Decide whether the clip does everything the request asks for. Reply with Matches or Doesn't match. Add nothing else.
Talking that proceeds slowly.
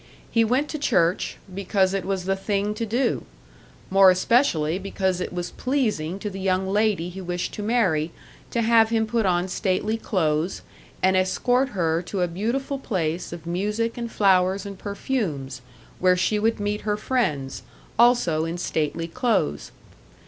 Doesn't match